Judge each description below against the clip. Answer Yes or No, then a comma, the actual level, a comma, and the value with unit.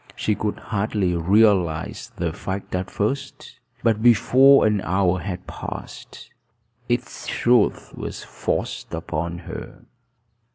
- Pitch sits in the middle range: No, low, 100 Hz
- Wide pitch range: No, average, 3.7 semitones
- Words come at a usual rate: No, slow, 115 wpm